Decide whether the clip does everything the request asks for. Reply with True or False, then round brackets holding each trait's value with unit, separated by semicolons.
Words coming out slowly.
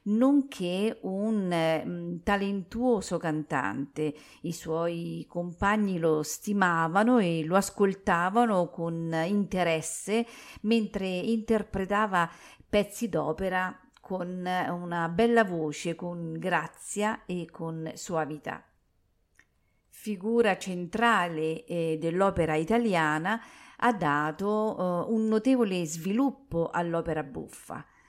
True (90 wpm)